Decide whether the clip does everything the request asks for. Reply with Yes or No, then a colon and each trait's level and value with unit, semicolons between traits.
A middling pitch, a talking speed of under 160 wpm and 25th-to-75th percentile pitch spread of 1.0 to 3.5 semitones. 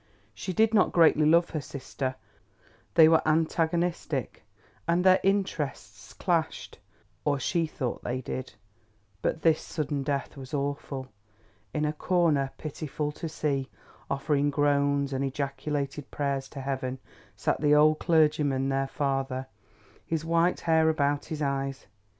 Yes: medium, 145 Hz; slow, 135 wpm; average, 2.8 semitones